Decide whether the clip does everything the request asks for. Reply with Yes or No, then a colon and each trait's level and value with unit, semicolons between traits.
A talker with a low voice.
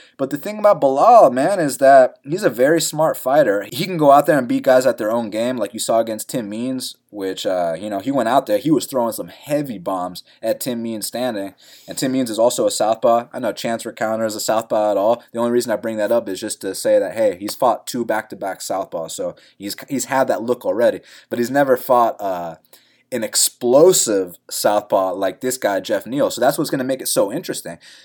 Yes: low, 125 Hz